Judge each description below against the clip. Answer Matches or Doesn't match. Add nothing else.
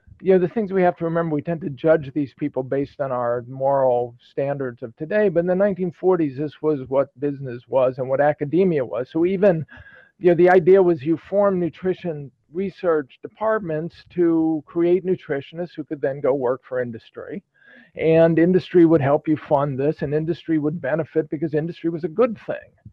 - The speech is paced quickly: Doesn't match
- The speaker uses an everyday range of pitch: Matches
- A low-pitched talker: Doesn't match